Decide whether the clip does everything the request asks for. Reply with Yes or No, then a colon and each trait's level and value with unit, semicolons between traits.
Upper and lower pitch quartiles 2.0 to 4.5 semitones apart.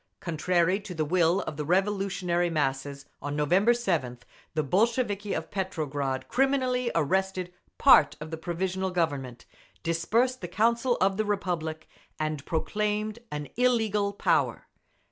No: average, 5.0 semitones